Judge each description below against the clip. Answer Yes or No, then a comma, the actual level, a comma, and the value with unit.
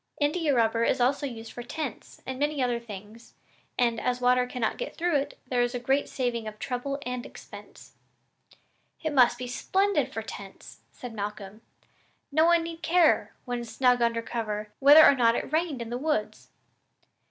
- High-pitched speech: Yes, very high, 250 Hz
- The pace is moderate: Yes, average, 175 wpm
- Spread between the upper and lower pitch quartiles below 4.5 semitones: Yes, average, 3.7 semitones